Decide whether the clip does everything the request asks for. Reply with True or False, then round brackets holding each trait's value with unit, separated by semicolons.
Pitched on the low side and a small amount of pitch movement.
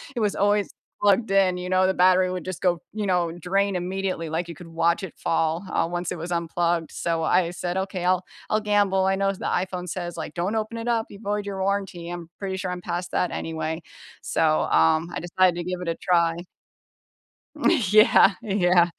False (180 Hz; 2.3 semitones)